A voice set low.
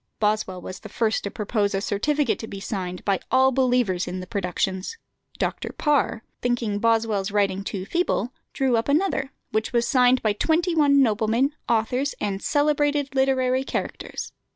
No: high, 230 Hz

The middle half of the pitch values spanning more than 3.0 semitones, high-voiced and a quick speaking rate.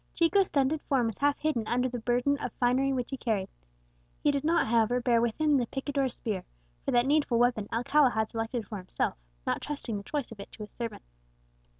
Yes: average, 3.8 semitones; high, 245 Hz; fast, 215 wpm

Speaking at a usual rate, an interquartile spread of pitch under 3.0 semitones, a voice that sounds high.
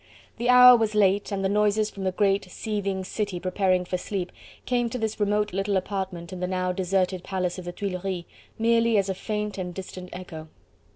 Yes: average, 195 wpm; narrow, 2.4 semitones; high, 195 Hz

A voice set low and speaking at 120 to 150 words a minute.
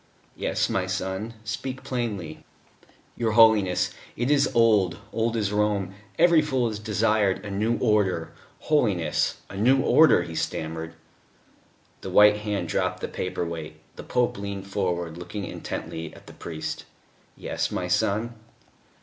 Yes: low, 105 Hz; average, 145 wpm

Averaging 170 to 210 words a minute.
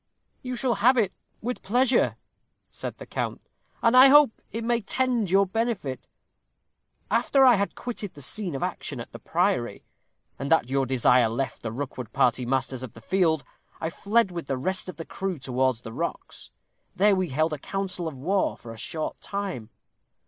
Yes: average, 185 wpm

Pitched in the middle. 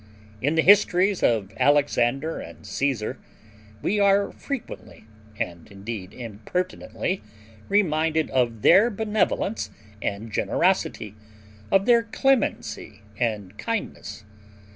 Yes: medium, 150 Hz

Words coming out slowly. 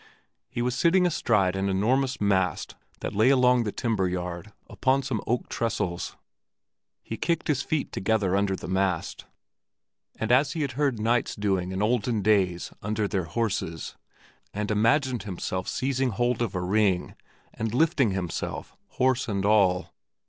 No: average, 155 wpm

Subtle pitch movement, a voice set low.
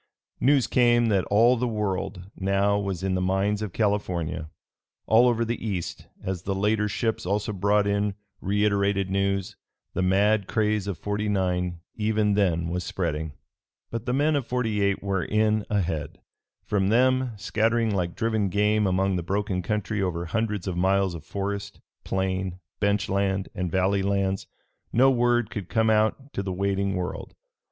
Yes: narrow, 2.3 semitones; low, 100 Hz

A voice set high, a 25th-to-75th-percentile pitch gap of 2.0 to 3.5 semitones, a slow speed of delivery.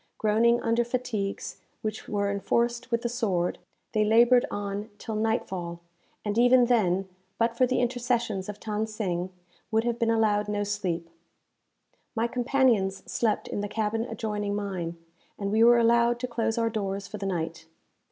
No: high, 220 Hz; average, 2.8 semitones; average, 165 wpm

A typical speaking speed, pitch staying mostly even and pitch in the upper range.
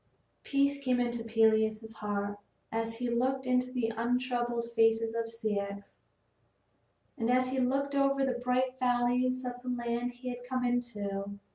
Yes: average, 150 wpm; narrow, 2.0 semitones; high, 245 Hz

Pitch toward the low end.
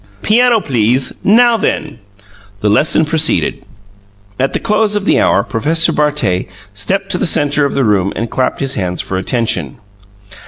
No: medium, 145 Hz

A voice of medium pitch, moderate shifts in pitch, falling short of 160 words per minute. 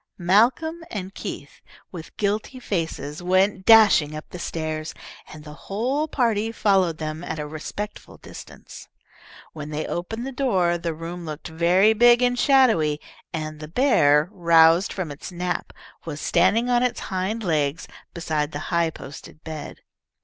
No: medium, 175 Hz; wide, 5.7 semitones; average, 150 wpm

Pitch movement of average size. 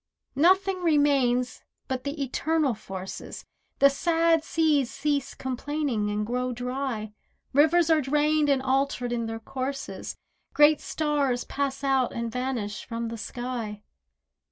Yes: average, 3.6 semitones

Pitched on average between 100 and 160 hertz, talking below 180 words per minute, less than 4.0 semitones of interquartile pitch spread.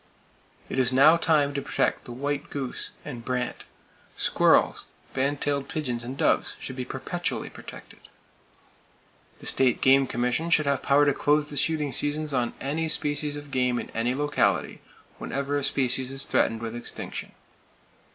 Yes: medium, 140 Hz; average, 160 wpm; narrow, 2.5 semitones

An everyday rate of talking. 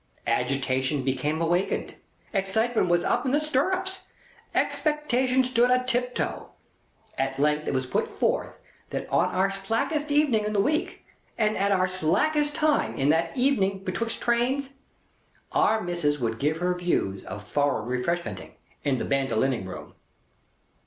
Yes: average, 145 wpm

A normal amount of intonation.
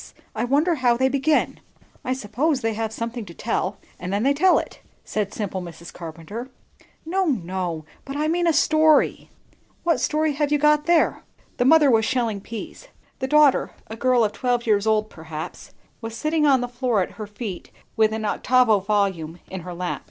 No: wide, 6.1 semitones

